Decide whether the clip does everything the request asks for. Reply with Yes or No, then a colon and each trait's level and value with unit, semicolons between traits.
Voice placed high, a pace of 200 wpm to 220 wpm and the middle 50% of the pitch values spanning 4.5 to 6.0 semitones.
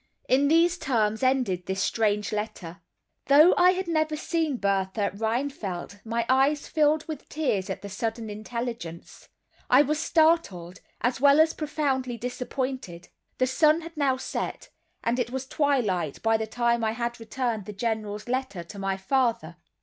No: high, 240 Hz; average, 155 wpm; wide, 5.4 semitones